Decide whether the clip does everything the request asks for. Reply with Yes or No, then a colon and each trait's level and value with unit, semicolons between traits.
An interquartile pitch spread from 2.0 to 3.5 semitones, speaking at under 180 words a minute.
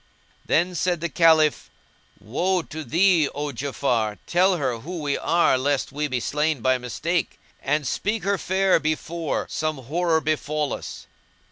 No: average, 3.9 semitones; average, 150 wpm